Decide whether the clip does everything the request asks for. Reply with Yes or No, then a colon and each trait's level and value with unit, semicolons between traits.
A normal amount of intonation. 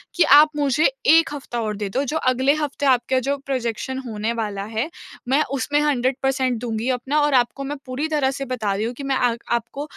Yes: average, 3.2 semitones